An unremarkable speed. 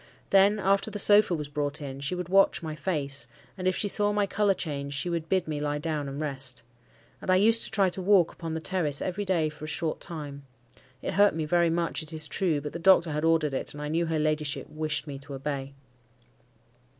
No: fast, 235 wpm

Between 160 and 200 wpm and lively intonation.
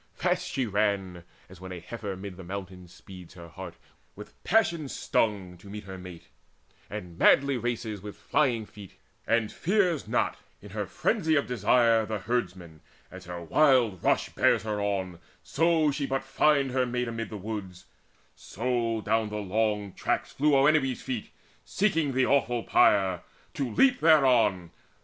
Yes: average, 165 wpm; wide, 6.0 semitones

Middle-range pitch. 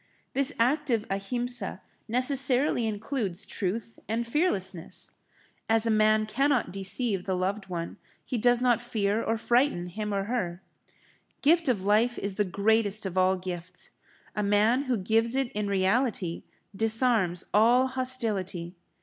No: high, 220 Hz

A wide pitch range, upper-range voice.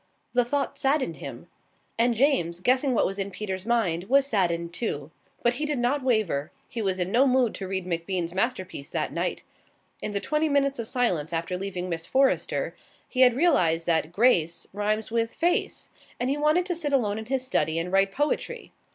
Yes: wide, 6.7 semitones; high, 220 Hz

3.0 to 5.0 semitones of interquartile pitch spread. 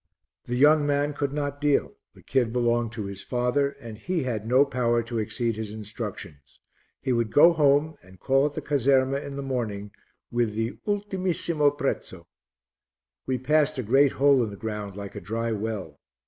Yes: average, 4.4 semitones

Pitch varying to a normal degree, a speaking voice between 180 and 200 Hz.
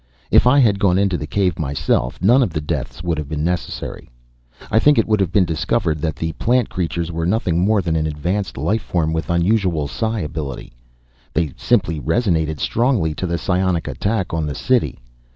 No: average, 4.4 semitones; very low, 85 Hz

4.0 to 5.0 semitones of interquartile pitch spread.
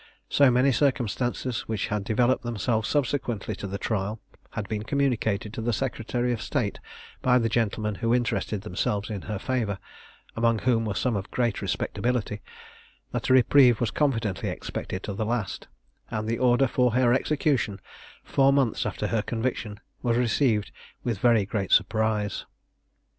No: average, 2.9 semitones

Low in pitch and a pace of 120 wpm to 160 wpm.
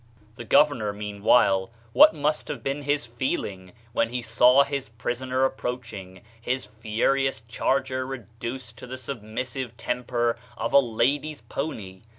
Yes: low, 125 Hz; average, 140 wpm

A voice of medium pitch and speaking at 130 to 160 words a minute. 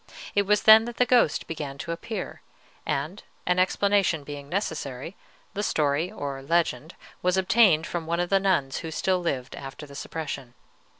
No: medium, 170 Hz; average, 170 wpm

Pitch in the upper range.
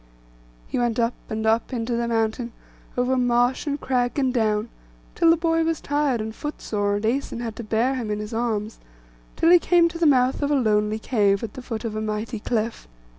Yes: high, 235 Hz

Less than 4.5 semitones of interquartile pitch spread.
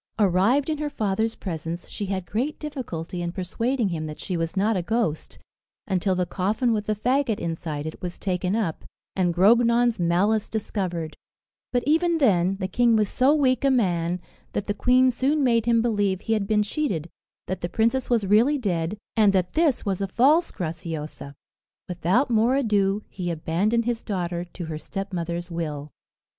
No: average, 5.3 semitones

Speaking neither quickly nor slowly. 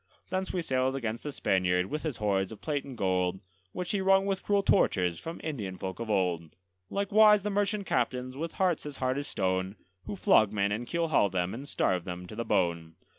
No: fast, 210 wpm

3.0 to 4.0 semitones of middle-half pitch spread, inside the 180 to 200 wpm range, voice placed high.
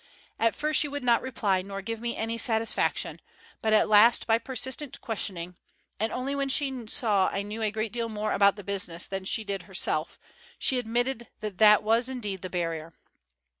Yes: average, 3.4 semitones; average, 190 wpm; high, 220 Hz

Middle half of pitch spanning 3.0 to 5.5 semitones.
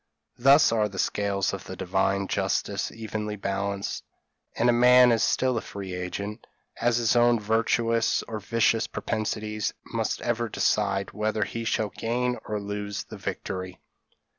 No: narrow, 2.5 semitones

